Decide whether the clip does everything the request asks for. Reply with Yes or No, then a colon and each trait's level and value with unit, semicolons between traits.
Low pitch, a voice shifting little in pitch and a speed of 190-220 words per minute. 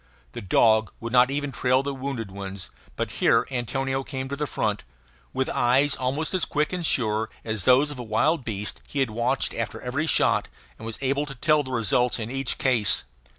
No: low, 130 Hz; average, 3.7 semitones; average, 200 wpm